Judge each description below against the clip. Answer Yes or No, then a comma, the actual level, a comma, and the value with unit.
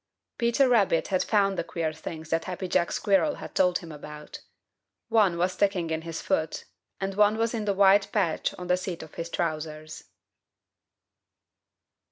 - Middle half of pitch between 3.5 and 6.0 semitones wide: Yes, average, 3.8 semitones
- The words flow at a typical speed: Yes, average, 170 wpm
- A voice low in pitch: No, medium, 180 Hz